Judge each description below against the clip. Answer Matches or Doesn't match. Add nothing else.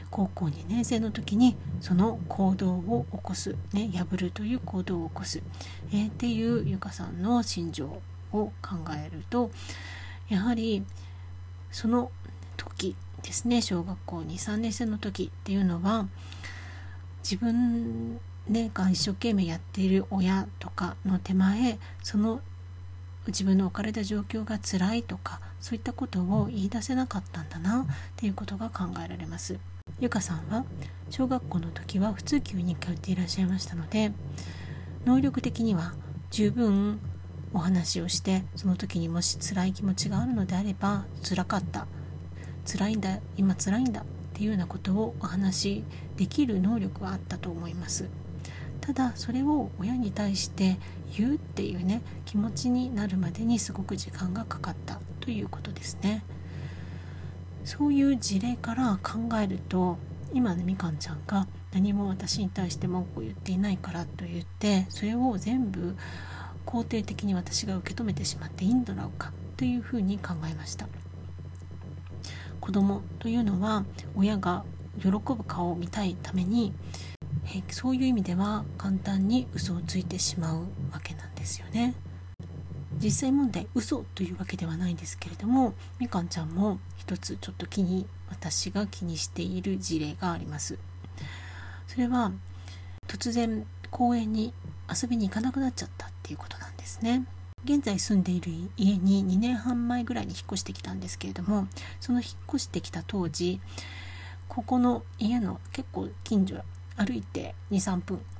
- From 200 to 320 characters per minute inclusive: Matches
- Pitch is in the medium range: Doesn't match